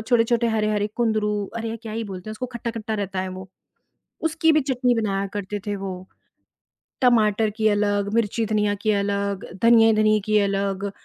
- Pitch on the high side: Yes, high, 215 Hz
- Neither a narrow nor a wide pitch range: No, narrow, 2.1 semitones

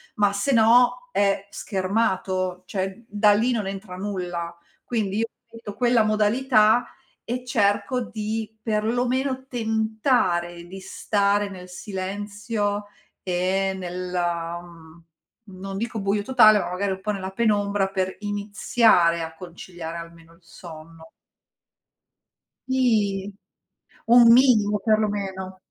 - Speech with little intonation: No, average, 3.1 semitones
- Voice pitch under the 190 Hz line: No, high, 205 Hz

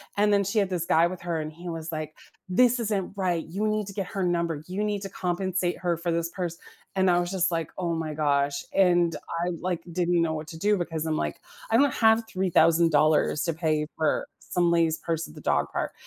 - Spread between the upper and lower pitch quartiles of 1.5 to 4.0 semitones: Yes, average, 2.8 semitones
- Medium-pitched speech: Yes, medium, 175 Hz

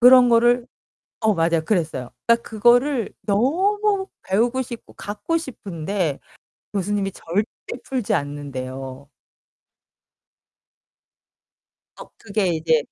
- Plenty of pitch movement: Yes, wide, 7.0 semitones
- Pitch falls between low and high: No, high, 205 Hz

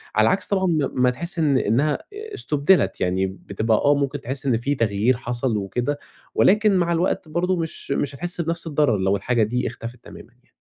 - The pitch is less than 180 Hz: Yes, medium, 140 Hz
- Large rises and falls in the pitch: Yes, wide, 6.3 semitones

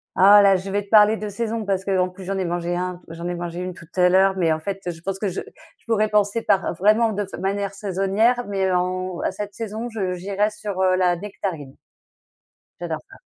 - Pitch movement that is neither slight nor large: No, narrow, 2.2 semitones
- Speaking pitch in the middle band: No, high, 195 Hz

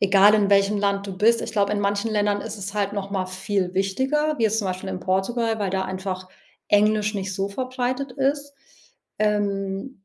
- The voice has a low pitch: No, high, 205 Hz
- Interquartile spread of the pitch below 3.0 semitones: Yes, narrow, 2.4 semitones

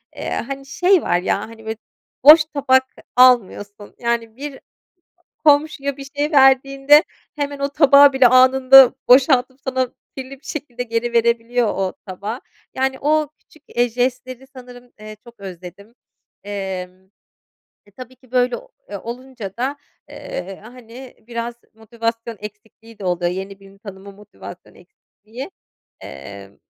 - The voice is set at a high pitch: Yes, high, 245 Hz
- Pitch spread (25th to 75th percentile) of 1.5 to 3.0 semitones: No, average, 4.2 semitones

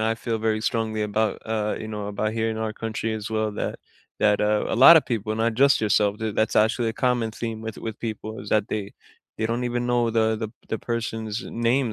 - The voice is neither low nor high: No, low, 110 Hz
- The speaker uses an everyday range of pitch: No, narrow, 1.2 semitones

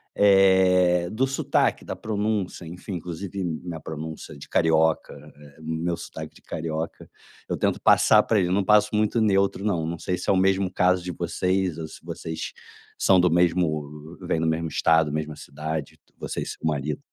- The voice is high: No, very low, 85 Hz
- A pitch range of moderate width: Yes, average, 3.2 semitones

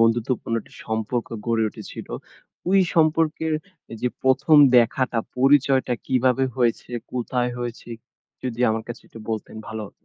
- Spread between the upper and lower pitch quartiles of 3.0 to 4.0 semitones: No, narrow, 2.6 semitones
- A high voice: No, low, 125 Hz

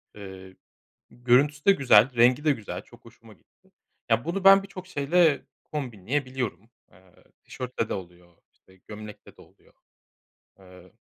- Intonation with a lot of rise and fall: Yes, wide, 7.4 semitones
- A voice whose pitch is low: Yes, low, 120 Hz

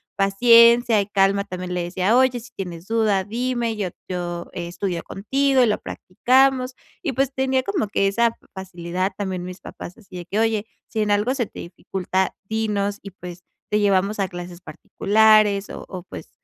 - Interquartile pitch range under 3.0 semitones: No, average, 4.0 semitones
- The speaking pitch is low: No, high, 205 Hz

